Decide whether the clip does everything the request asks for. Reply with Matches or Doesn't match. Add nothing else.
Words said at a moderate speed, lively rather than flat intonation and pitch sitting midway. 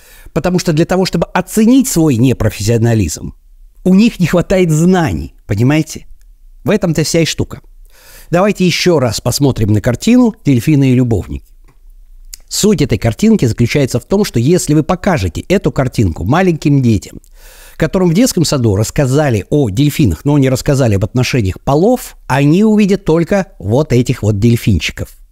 Matches